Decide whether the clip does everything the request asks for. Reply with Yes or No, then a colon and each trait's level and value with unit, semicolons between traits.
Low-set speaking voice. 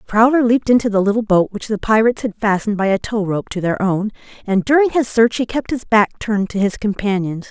No: high, 215 Hz